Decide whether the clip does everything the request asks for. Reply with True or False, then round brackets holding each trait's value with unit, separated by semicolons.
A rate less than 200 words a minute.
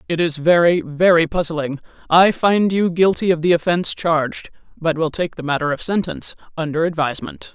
True (175 wpm)